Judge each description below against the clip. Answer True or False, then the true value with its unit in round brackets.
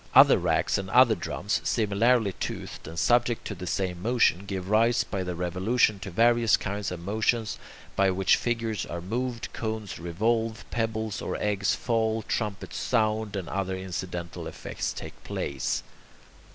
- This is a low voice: True (105 Hz)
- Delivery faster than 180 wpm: False (150 wpm)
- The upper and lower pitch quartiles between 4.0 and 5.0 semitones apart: False (3.4 semitones)